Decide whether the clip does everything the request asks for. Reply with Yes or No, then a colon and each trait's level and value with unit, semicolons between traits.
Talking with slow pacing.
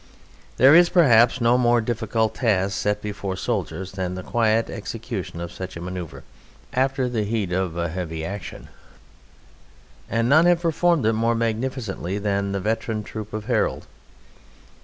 No: average, 155 wpm